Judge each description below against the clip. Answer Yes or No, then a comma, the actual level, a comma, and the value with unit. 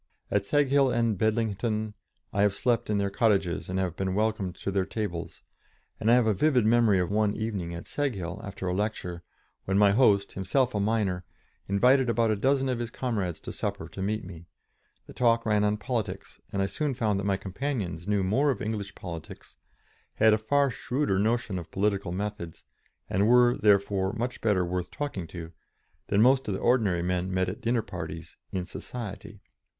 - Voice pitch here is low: Yes, low, 105 Hz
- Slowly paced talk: No, average, 190 wpm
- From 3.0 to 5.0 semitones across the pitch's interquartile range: Yes, average, 3.6 semitones